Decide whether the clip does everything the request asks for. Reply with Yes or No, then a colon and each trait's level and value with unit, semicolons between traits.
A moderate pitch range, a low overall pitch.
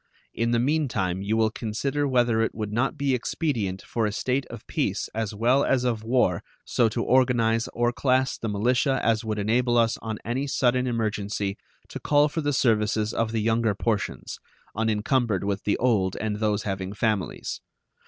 Yes: average, 3.0 semitones; low, 115 Hz